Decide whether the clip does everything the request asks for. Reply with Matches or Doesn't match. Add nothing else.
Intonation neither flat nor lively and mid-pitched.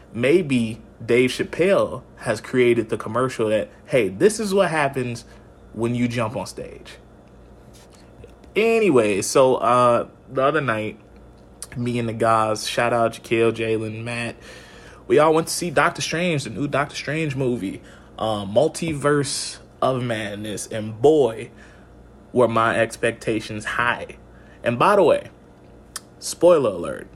Doesn't match